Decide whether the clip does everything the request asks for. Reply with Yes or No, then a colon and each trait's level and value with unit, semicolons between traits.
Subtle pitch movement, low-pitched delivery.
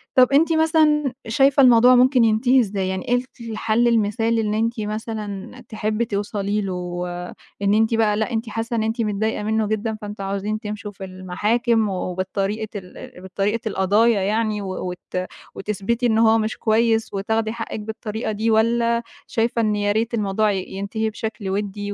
No: narrow, 2.2 semitones; high, 220 Hz